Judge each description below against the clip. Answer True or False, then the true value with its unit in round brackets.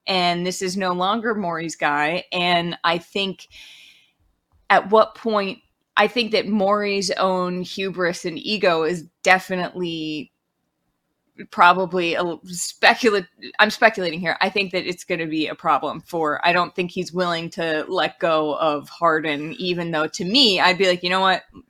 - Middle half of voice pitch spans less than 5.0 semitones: True (2.5 semitones)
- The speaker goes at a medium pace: True (165 wpm)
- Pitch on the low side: False (180 Hz)